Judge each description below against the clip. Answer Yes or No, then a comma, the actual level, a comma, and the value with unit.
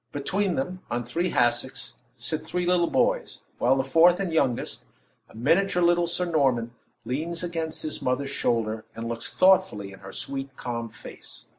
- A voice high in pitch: No, medium, 140 Hz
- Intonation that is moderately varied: No, wide, 6.4 semitones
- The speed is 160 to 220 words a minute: Yes, average, 165 wpm